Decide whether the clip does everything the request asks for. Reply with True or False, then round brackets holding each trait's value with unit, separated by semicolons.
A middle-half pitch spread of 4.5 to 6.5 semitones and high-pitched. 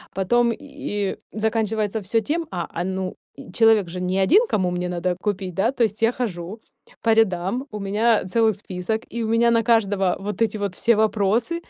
False (3.3 semitones; 210 Hz)